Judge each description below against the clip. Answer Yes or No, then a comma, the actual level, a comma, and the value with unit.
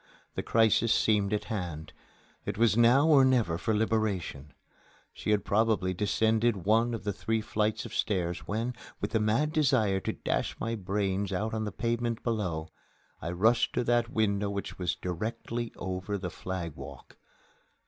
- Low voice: Yes, low, 105 Hz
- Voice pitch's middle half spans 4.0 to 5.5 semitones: No, average, 3.6 semitones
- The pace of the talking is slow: No, average, 160 wpm